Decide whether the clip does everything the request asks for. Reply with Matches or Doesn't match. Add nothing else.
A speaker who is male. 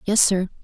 Doesn't match